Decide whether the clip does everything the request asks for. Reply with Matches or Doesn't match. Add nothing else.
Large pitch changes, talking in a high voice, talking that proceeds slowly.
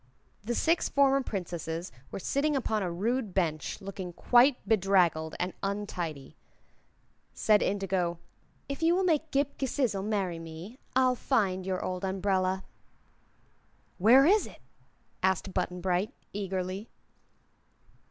Matches